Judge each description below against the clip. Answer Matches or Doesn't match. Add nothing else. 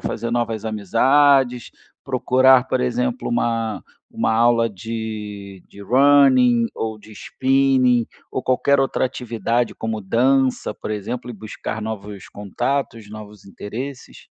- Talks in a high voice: Doesn't match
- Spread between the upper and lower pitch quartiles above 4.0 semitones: Doesn't match